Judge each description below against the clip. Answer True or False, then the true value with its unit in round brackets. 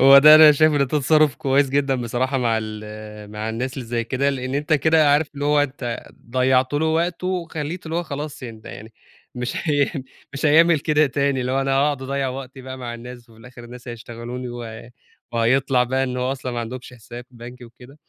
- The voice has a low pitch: True (130 Hz)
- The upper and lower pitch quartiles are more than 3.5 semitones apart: False (3.1 semitones)